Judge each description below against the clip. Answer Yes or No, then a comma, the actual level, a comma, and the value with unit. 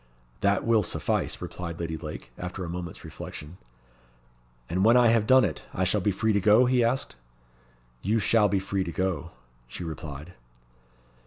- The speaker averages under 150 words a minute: No, average, 170 wpm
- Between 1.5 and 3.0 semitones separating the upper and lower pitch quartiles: No, average, 4.4 semitones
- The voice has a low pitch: Yes, very low, 95 Hz